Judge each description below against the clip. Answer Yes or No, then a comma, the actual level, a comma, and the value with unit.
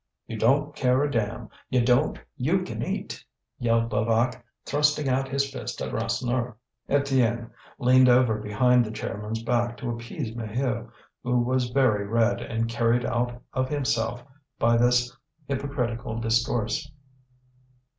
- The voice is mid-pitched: No, low, 120 Hz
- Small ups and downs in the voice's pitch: Yes, narrow, 2.0 semitones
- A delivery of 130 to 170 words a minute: Yes, slow, 135 wpm